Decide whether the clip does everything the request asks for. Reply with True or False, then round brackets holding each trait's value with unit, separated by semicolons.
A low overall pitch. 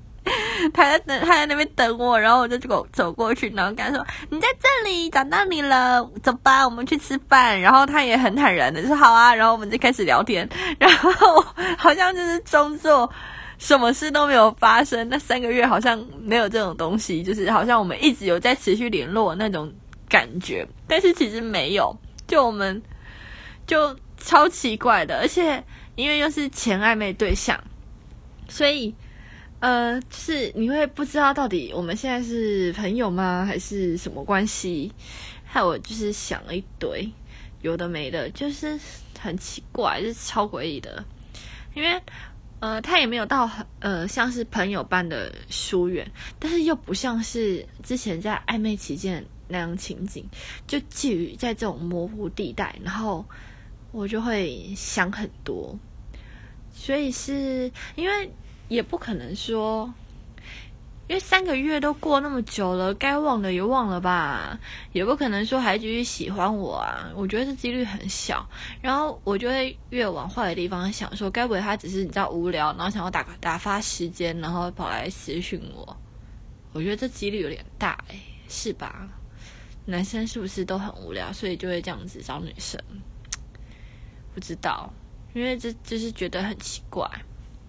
False (230 Hz)